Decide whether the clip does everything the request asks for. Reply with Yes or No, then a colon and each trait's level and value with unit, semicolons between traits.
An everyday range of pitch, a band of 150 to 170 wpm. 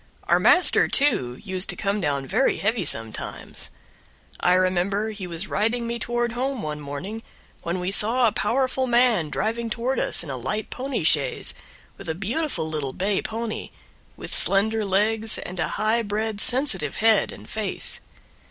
Yes: average, 4.5 semitones; average, 165 wpm